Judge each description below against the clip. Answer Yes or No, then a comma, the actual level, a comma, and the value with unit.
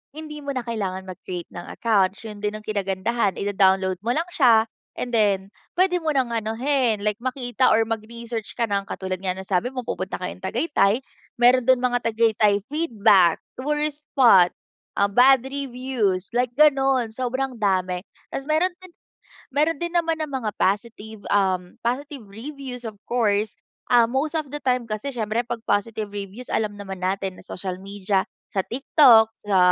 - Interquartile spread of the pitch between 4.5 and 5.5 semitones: Yes, average, 4.8 semitones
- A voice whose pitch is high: Yes, high, 225 Hz